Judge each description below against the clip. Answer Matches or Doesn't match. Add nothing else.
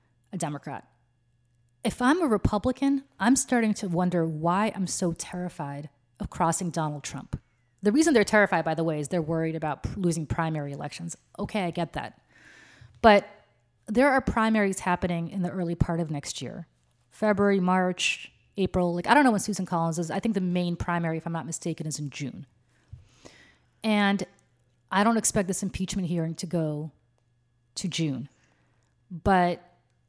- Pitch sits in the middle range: Matches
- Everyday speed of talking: Matches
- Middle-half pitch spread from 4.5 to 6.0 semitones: Matches